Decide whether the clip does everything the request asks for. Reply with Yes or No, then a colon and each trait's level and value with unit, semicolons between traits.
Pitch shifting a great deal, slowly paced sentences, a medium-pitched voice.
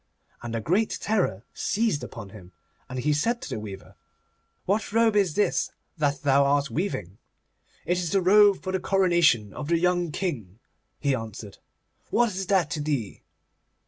No: wide, 8.4 semitones; average, 170 wpm; medium, 155 Hz